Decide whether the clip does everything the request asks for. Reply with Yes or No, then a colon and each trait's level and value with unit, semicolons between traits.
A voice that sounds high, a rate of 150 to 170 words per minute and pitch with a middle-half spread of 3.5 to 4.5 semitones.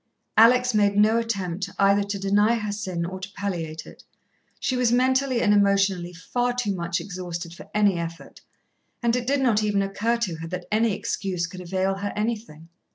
No: high, 200 Hz; average, 185 wpm; average, 3.9 semitones